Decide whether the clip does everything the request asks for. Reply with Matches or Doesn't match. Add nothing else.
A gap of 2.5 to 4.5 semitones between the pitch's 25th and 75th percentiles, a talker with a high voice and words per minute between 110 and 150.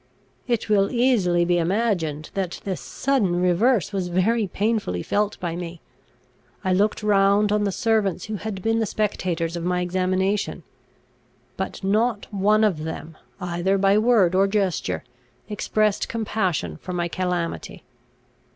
Matches